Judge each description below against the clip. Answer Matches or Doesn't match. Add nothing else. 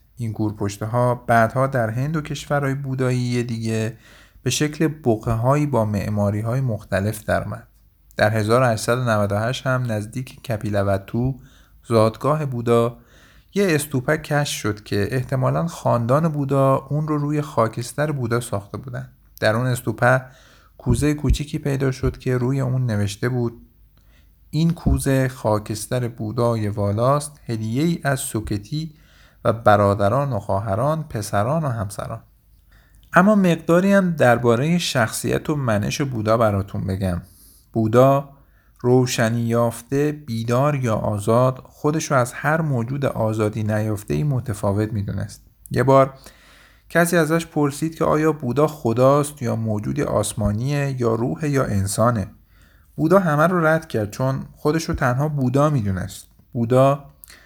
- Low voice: Matches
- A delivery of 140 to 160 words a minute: Doesn't match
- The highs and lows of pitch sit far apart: Doesn't match